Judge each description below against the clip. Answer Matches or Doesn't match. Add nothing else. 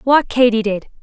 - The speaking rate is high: Doesn't match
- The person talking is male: Doesn't match